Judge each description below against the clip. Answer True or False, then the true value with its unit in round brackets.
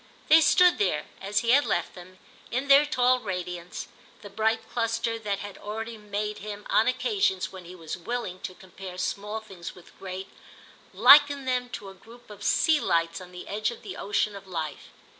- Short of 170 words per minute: False (190 wpm)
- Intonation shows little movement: False (4.4 semitones)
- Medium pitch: False (210 Hz)